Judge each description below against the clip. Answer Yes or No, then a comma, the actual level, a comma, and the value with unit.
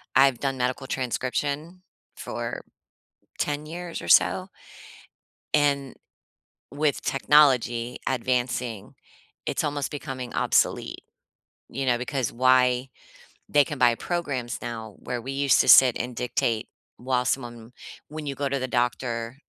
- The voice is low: Yes, low, 130 Hz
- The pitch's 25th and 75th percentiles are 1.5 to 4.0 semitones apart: Yes, narrow, 2.6 semitones